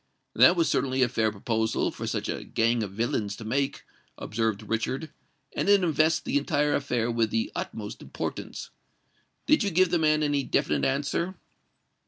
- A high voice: No, low, 135 Hz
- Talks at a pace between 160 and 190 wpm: Yes, average, 170 wpm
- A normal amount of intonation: No, wide, 6.0 semitones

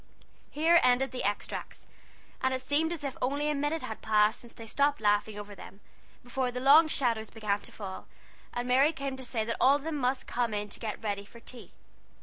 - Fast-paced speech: Yes, fast, 215 wpm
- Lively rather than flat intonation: No, average, 4.4 semitones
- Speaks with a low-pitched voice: No, very high, 250 Hz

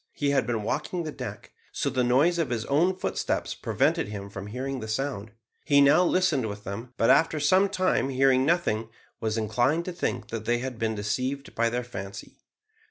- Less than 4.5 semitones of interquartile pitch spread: No, average, 5.1 semitones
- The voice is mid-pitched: No, low, 130 Hz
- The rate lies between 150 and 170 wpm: No, average, 195 wpm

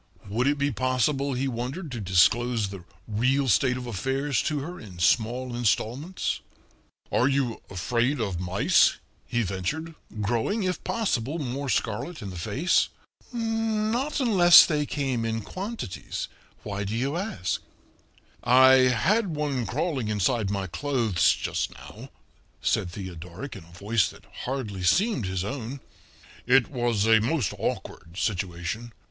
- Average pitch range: No, wide, 5.8 semitones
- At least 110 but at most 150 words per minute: Yes, average, 140 wpm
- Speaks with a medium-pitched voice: No, low, 125 Hz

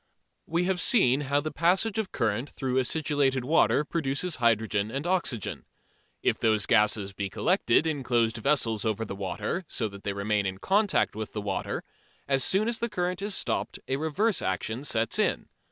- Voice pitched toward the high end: No, low, 130 Hz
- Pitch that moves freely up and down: Yes, wide, 7.7 semitones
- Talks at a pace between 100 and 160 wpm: No, average, 180 wpm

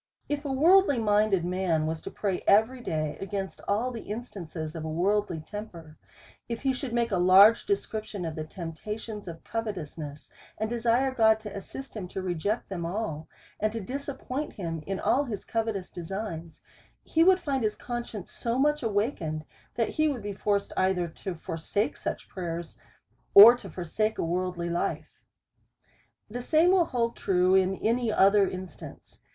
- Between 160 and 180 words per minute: Yes, average, 170 wpm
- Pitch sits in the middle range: No, high, 205 Hz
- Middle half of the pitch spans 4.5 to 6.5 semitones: Yes, average, 5.0 semitones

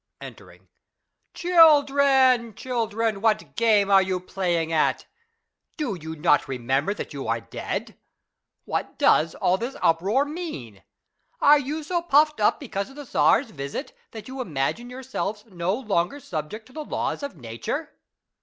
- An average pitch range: No, wide, 8.1 semitones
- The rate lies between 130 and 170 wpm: Yes, average, 150 wpm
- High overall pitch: Yes, high, 220 Hz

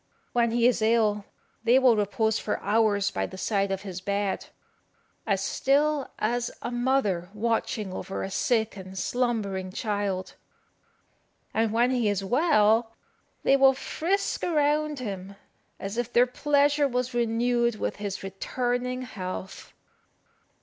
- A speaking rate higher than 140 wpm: No, slow, 135 wpm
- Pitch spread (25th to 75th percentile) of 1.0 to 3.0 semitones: No, average, 3.9 semitones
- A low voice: No, high, 225 Hz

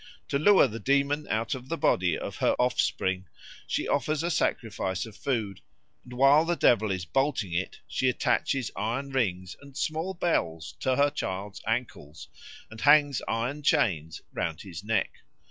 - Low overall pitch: Yes, low, 120 Hz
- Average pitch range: No, wide, 6.9 semitones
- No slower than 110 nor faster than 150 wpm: No, average, 165 wpm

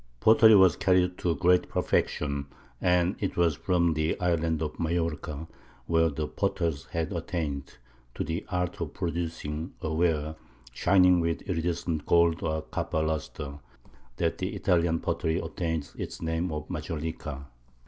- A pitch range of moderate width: No, narrow, 2.1 semitones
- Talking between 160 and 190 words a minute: No, average, 140 wpm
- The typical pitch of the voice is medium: No, very low, 80 Hz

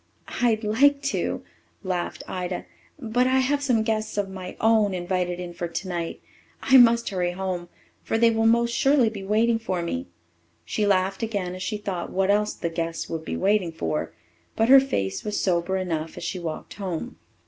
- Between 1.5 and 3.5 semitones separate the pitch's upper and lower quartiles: No, average, 4.2 semitones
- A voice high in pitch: Yes, high, 195 Hz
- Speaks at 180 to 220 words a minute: Yes, average, 185 wpm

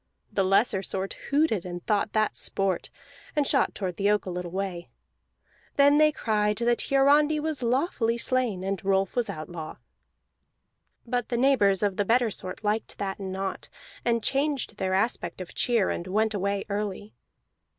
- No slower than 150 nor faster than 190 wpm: Yes, average, 160 wpm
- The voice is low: No, high, 210 Hz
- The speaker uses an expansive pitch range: No, average, 4.2 semitones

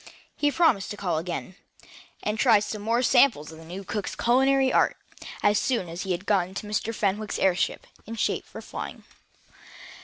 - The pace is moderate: Yes, average, 175 wpm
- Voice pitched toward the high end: Yes, high, 210 Hz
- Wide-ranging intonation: No, average, 4.2 semitones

